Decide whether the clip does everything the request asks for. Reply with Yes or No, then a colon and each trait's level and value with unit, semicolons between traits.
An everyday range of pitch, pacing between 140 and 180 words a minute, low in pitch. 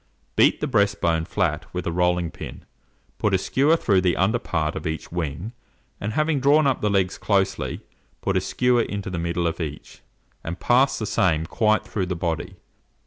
No: average, 4.5 semitones; average, 195 wpm; very low, 95 Hz